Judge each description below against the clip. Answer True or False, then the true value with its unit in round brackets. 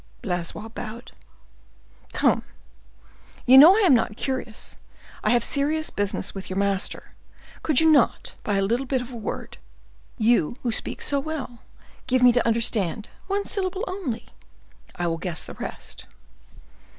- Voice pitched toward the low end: False (240 Hz)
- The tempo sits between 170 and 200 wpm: False (135 wpm)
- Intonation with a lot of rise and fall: True (5.7 semitones)